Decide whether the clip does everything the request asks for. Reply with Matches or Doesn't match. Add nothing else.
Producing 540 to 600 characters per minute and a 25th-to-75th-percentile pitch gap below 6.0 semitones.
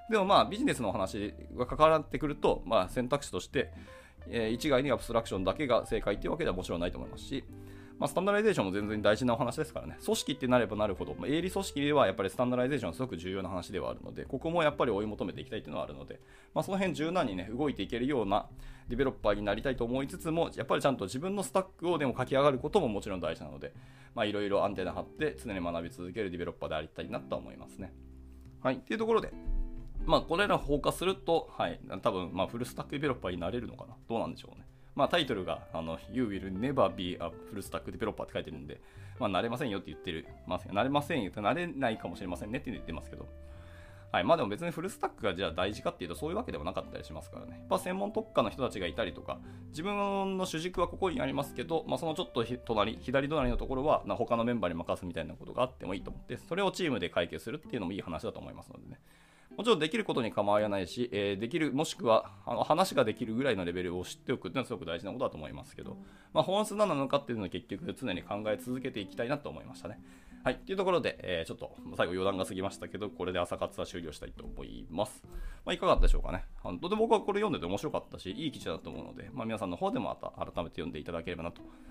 Doesn't match